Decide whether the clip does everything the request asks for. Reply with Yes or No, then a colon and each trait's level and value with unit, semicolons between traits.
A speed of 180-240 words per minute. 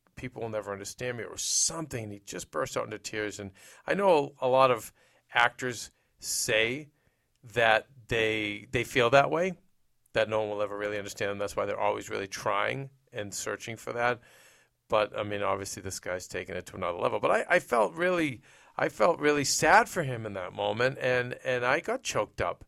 Yes: average, 200 wpm